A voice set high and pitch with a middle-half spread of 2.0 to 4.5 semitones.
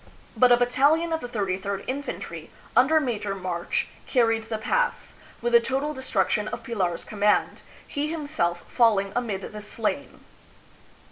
No: high, 235 Hz; average, 5.0 semitones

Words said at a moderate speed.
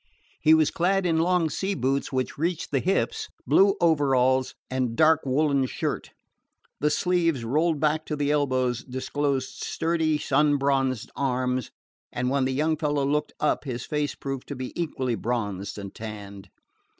Yes: average, 160 wpm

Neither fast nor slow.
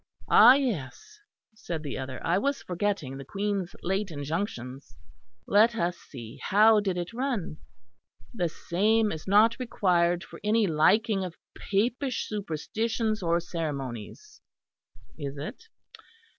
No: slow, 125 wpm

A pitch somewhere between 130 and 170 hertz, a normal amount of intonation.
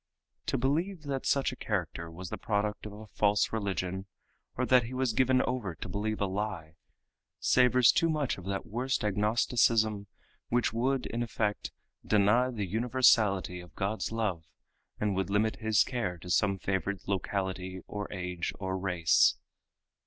No: low, 105 Hz; average, 4.0 semitones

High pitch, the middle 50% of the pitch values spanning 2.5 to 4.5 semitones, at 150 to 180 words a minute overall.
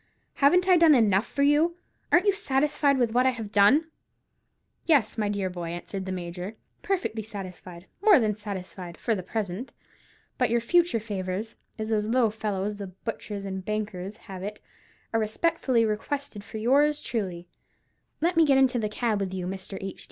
No: high, 215 Hz; wide, 5.6 semitones; average, 165 wpm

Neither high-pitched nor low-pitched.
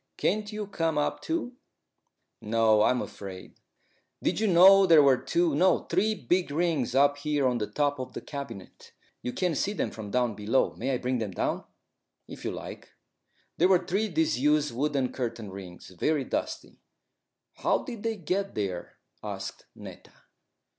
Yes: medium, 145 Hz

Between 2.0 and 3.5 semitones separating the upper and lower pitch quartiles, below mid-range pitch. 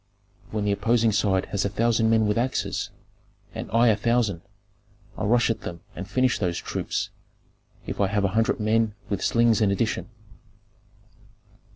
Yes: narrow, 2.4 semitones; low, 110 Hz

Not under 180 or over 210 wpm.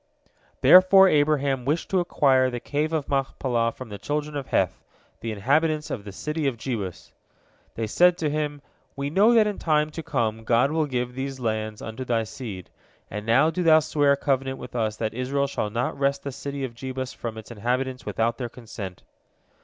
Yes: average, 195 wpm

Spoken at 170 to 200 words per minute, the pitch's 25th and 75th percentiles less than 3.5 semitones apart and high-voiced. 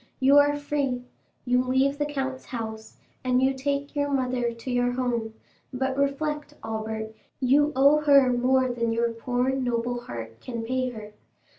No: average, 160 wpm; average, 2.8 semitones; very high, 255 Hz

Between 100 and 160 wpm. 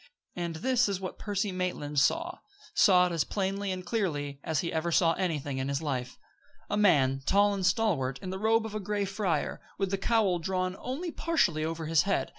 No: fast, 205 wpm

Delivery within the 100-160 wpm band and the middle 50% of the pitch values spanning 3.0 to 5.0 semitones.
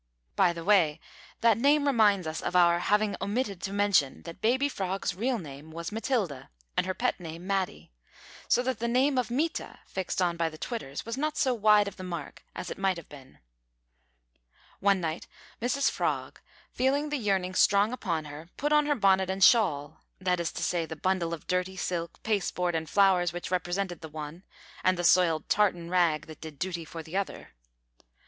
No: average, 195 wpm; average, 4.2 semitones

